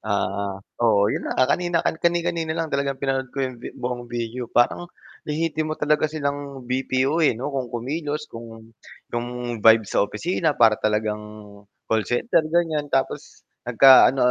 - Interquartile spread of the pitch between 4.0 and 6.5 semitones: Yes, average, 4.7 semitones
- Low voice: Yes, low, 130 Hz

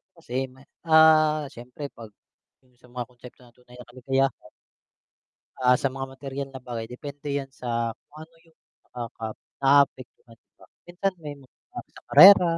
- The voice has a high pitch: No, low, 135 Hz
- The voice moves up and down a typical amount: Yes, average, 3.1 semitones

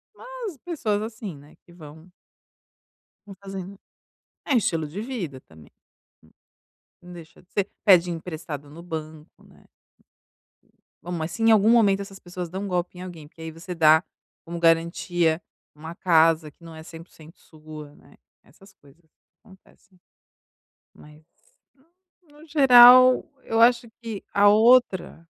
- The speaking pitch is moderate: Yes, medium, 175 Hz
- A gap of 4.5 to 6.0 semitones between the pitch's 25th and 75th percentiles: Yes, average, 4.8 semitones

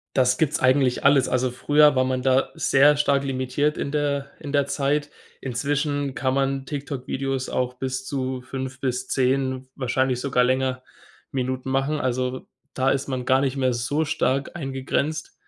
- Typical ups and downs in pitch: No, narrow, 1.6 semitones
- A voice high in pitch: No, low, 135 Hz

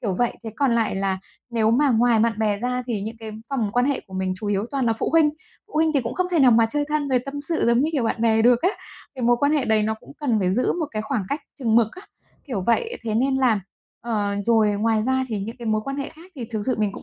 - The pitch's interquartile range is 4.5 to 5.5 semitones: No, average, 3.9 semitones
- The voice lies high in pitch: Yes, high, 235 Hz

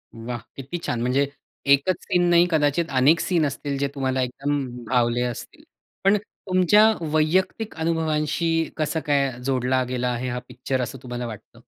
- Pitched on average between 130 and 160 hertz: Yes, medium, 140 Hz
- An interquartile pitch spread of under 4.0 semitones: No, average, 4.3 semitones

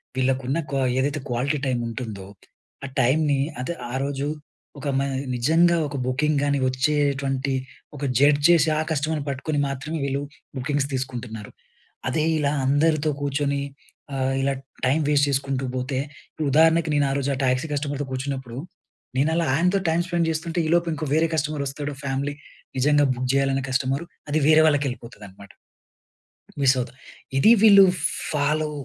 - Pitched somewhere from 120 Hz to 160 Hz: Yes, medium, 140 Hz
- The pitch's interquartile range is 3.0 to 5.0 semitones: No, narrow, 2.5 semitones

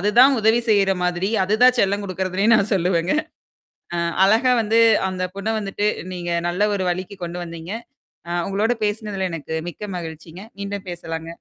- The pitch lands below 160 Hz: No, high, 195 Hz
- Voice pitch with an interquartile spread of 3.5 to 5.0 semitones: No, average, 3.0 semitones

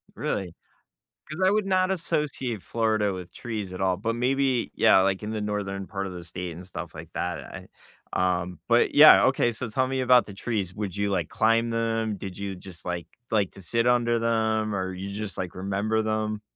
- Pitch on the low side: Yes, low, 105 Hz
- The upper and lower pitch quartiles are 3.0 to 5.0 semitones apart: Yes, average, 3.5 semitones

